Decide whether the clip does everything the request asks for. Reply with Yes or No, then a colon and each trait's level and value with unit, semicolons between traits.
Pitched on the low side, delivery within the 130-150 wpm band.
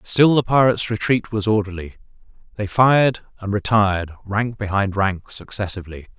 Yes: low, 105 Hz; slow, 135 wpm